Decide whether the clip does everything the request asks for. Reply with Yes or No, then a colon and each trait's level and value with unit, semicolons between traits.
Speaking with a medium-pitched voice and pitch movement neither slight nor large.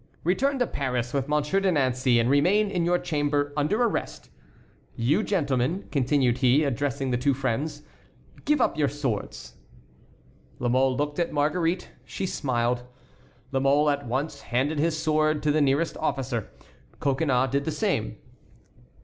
Yes: medium, 145 Hz; average, 3.5 semitones